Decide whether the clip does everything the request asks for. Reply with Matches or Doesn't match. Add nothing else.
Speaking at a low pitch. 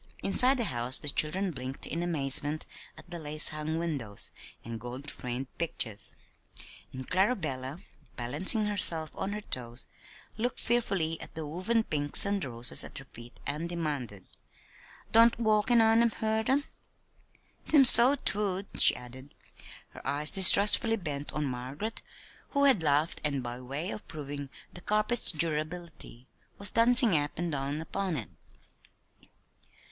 Doesn't match